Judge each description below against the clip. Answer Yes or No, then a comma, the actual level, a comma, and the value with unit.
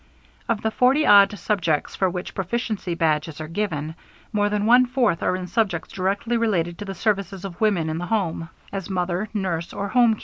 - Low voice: No, high, 195 Hz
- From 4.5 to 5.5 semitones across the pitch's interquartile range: No, average, 3.9 semitones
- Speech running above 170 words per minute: Yes, average, 200 wpm